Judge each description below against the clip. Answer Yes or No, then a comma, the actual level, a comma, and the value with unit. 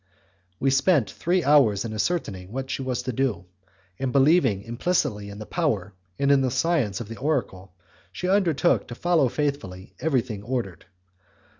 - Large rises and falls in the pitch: Yes, wide, 6.3 semitones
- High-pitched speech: No, low, 130 Hz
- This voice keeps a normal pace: Yes, average, 160 wpm